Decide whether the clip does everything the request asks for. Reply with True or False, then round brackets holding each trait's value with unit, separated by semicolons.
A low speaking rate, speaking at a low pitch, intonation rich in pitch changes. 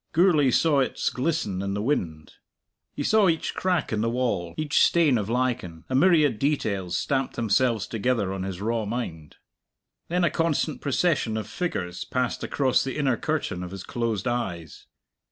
False (170 wpm; 125 Hz; 6.9 semitones)